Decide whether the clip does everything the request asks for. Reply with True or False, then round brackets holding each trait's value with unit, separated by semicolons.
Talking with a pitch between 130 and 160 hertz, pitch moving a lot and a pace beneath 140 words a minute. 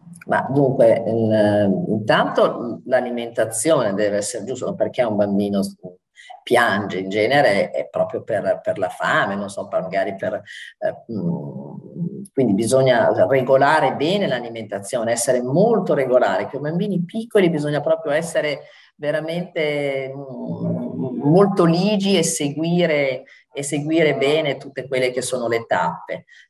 True (140 Hz; 6.9 semitones; 120 wpm)